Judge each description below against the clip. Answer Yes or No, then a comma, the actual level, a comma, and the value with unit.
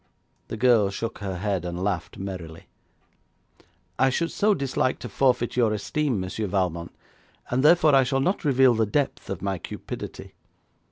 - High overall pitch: No, low, 115 Hz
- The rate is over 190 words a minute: No, average, 160 wpm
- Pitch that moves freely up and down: Yes, wide, 5.7 semitones